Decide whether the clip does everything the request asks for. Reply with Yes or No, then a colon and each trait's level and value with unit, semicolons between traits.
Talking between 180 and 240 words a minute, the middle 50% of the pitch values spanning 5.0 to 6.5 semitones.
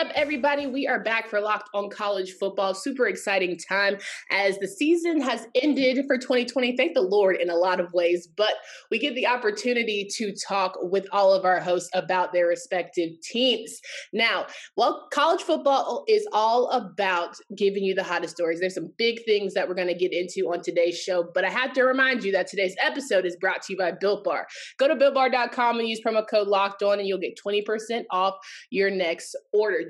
Yes: fast, 205 wpm; average, 5.3 semitones